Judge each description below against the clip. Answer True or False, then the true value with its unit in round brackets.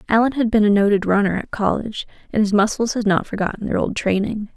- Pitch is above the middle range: True (210 Hz)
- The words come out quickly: True (225 wpm)